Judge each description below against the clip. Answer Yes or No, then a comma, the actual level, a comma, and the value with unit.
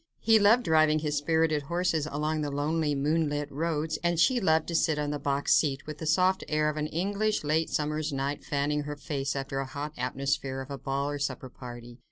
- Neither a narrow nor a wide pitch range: No, narrow, 2.2 semitones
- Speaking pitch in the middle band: Yes, medium, 150 Hz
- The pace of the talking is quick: Yes, fast, 215 wpm